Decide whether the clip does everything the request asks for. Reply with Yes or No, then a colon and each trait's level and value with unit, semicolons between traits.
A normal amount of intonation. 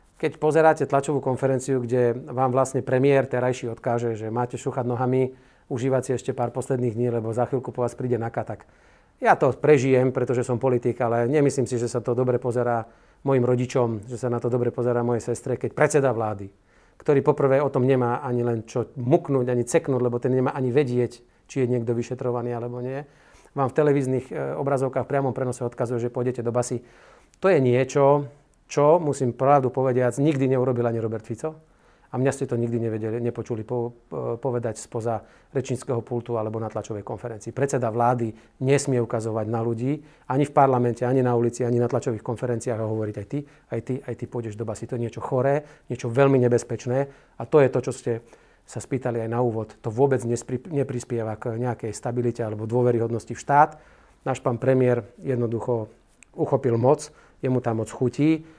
No: narrow, 2.0 semitones